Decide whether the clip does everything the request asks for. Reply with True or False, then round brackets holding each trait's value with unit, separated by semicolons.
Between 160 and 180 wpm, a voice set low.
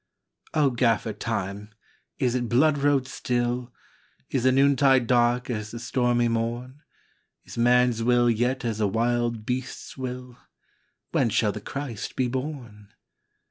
False (150 wpm; 120 Hz)